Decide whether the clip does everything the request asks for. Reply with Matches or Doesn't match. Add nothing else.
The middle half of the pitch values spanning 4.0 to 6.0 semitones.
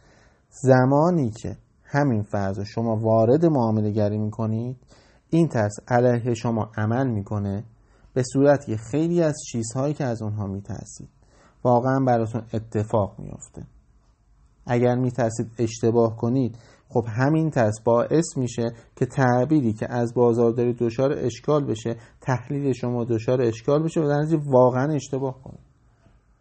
Doesn't match